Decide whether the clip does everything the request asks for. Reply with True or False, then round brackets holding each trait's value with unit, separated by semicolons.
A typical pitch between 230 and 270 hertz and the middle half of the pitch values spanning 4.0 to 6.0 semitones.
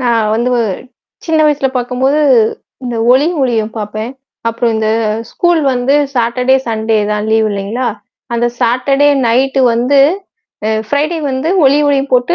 False (245 Hz; 3.1 semitones)